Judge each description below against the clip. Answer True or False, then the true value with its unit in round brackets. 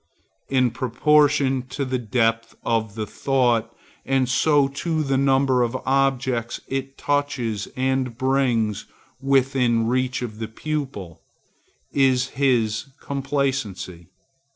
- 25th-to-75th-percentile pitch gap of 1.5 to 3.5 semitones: True (2.9 semitones)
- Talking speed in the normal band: False (115 wpm)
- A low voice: True (130 Hz)